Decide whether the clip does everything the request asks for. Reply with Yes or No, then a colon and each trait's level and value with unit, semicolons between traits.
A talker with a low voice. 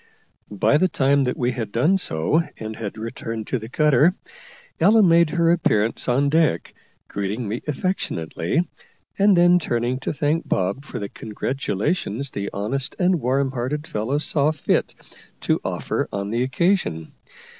Yes: low, 130 Hz